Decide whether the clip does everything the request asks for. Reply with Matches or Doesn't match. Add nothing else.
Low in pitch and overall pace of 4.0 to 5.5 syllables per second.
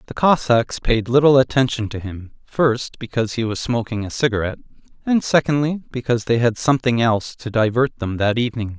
Doesn't match